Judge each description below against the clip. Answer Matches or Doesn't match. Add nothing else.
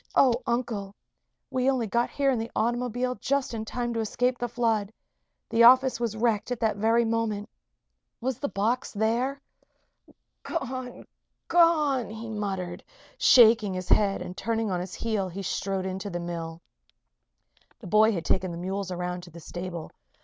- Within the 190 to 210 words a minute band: Doesn't match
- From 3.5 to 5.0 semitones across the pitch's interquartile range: Matches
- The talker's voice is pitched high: Matches